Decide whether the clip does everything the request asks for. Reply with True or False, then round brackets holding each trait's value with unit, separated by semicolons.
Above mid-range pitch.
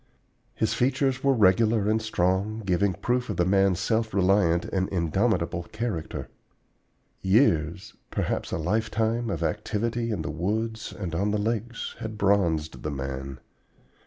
False (100 Hz)